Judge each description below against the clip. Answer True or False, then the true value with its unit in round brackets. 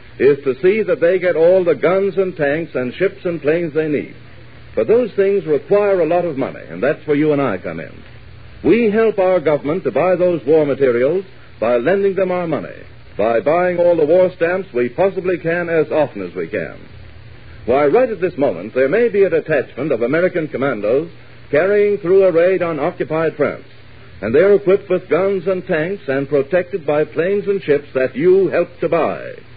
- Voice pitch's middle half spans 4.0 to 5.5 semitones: True (4.8 semitones)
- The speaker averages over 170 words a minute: True (205 wpm)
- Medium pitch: True (180 Hz)